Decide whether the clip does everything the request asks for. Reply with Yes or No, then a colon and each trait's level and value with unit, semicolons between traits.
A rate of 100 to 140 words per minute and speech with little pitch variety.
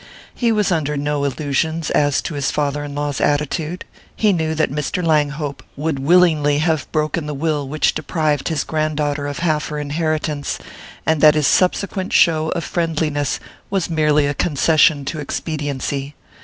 No: average, 165 wpm; narrow, 1.9 semitones